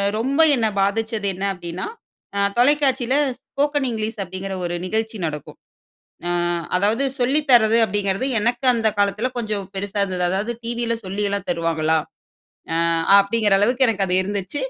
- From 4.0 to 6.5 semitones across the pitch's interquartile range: No, average, 3.6 semitones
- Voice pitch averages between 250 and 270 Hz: No, high, 210 Hz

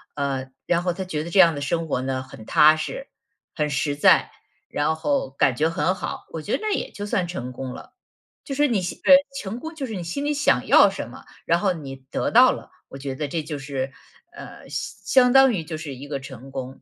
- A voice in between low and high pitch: Yes, medium, 155 Hz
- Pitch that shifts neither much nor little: No, wide, 5.7 semitones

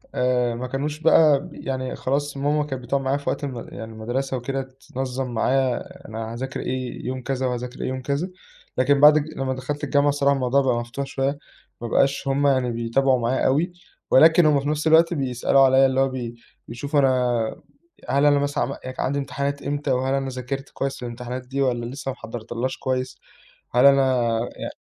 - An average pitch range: No, narrow, 1.9 semitones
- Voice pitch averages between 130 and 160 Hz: Yes, low, 135 Hz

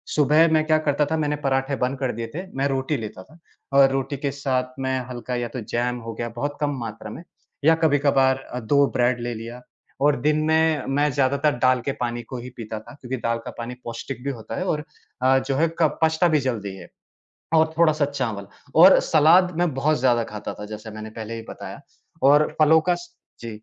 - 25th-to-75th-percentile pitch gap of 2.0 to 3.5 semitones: No, average, 4.1 semitones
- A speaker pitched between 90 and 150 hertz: Yes, low, 135 Hz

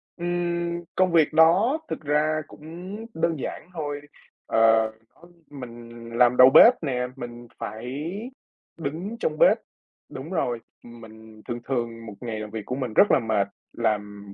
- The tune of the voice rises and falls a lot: Yes, wide, 6.3 semitones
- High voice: No, low, 130 Hz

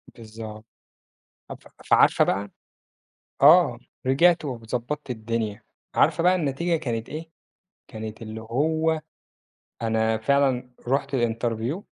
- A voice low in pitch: Yes, low, 125 Hz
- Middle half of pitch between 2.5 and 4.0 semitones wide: No, average, 5.0 semitones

